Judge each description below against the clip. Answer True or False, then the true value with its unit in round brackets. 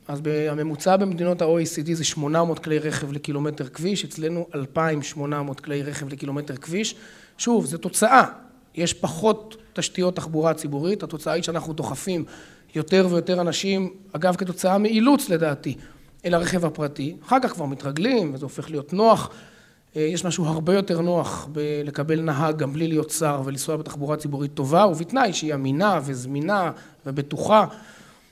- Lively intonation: False (3.5 semitones)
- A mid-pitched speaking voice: True (160 Hz)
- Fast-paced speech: False (140 wpm)